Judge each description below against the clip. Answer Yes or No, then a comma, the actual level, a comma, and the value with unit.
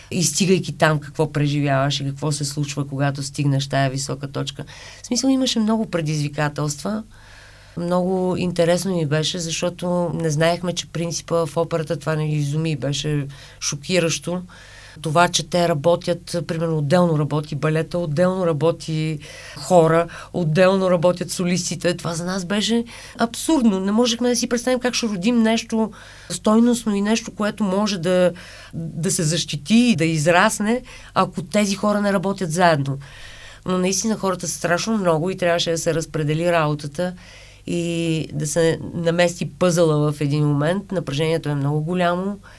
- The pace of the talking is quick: No, average, 150 wpm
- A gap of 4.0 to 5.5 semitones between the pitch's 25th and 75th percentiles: No, average, 3.4 semitones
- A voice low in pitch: No, medium, 170 Hz